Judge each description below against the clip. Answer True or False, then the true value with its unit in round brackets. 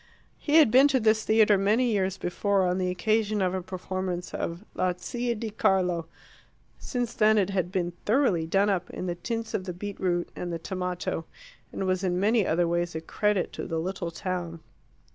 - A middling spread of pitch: True (3.4 semitones)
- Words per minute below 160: False (200 wpm)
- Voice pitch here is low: False (190 Hz)